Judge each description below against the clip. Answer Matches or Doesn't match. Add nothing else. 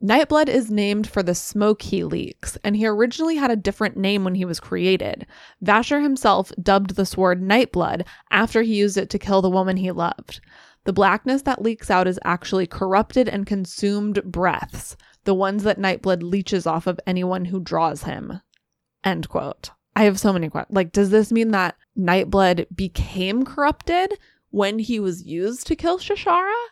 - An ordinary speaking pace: Matches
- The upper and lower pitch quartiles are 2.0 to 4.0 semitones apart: Matches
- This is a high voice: Matches